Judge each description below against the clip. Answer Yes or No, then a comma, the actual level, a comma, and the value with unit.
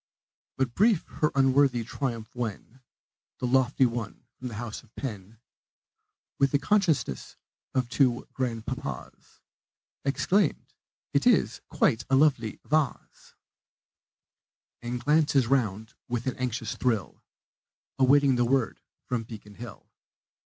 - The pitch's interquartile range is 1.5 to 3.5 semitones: Yes, average, 3.1 semitones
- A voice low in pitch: Yes, low, 125 Hz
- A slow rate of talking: Yes, slow, 115 wpm